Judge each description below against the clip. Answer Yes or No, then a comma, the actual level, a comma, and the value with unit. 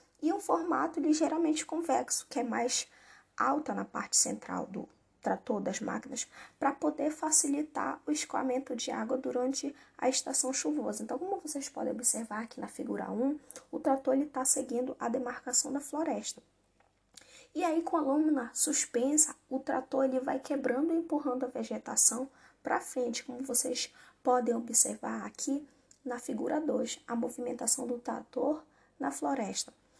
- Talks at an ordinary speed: Yes, average, 150 wpm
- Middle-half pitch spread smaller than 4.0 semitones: Yes, average, 3.0 semitones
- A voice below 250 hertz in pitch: No, very high, 265 Hz